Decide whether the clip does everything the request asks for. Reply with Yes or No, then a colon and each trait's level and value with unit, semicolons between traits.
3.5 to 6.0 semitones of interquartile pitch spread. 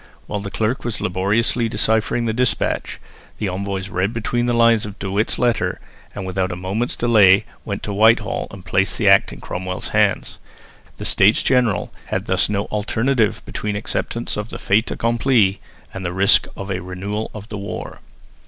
No: average, 3.1 semitones